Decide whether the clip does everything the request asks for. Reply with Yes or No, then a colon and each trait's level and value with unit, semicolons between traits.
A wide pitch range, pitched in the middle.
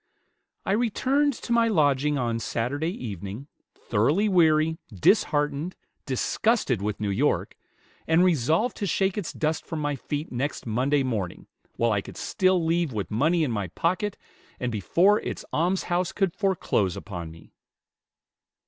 Yes: wide, 7.8 semitones; medium, 150 Hz